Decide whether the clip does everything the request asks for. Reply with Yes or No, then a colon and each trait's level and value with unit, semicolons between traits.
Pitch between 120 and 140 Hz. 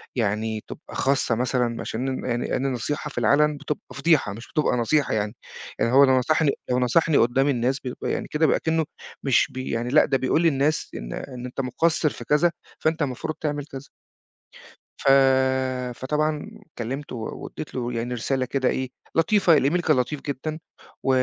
Yes: low, 135 Hz